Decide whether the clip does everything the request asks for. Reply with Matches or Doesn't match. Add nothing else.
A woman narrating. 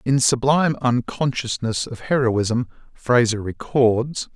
Doesn't match